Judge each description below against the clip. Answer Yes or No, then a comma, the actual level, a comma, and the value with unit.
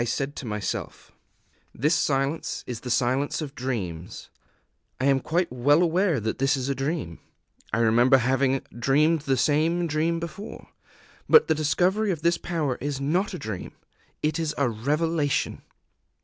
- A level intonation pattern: No, average, 4.4 semitones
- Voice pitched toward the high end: No, medium, 140 Hz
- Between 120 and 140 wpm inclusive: No, average, 160 wpm